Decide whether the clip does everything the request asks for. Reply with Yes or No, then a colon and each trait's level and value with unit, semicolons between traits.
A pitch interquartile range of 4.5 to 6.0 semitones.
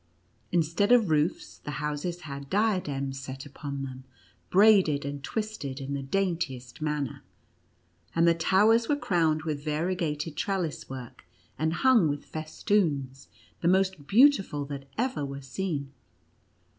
Yes: average, 5.2 semitones